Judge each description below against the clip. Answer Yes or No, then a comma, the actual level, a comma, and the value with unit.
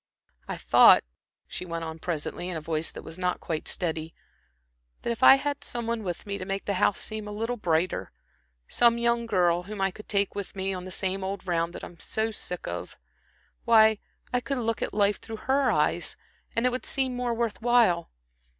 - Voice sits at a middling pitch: No, high, 200 Hz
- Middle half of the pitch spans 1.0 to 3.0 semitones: No, average, 4.6 semitones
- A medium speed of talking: No, fast, 210 wpm